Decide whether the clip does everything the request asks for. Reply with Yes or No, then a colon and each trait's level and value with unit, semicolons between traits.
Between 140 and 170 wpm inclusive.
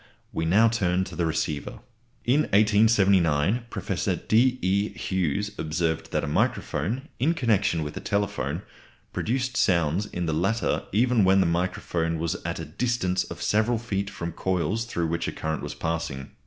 Yes: average, 165 wpm